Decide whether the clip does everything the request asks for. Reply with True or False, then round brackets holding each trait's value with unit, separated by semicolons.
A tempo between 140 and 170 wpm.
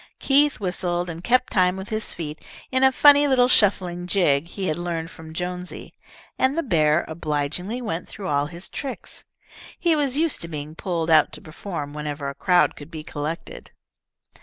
False (180 wpm)